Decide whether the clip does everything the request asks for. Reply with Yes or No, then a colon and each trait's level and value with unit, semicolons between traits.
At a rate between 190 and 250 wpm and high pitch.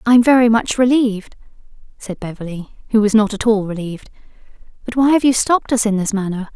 Yes: average, 200 wpm; high, 220 Hz